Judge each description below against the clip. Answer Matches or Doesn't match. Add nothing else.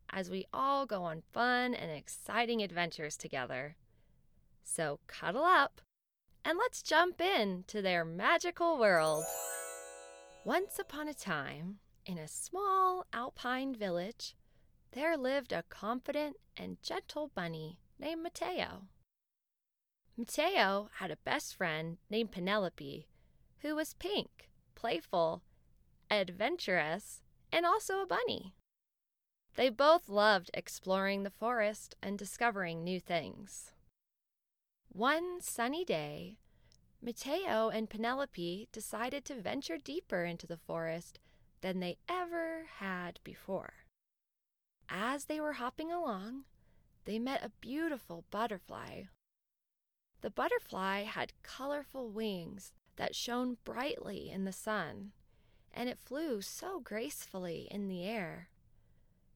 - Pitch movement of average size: Doesn't match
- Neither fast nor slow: Doesn't match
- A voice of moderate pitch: Doesn't match